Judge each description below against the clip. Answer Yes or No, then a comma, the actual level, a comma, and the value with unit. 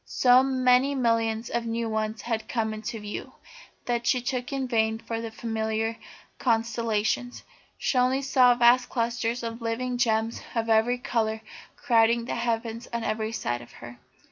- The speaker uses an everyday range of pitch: No, narrow, 1.7 semitones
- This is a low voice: No, high, 230 Hz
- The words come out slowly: No, average, 160 wpm